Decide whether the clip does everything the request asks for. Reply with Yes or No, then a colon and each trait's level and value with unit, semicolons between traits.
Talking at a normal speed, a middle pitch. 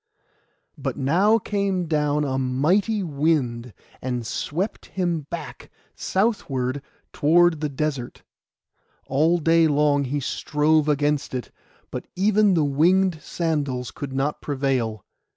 No: slow, 115 wpm; medium, 150 Hz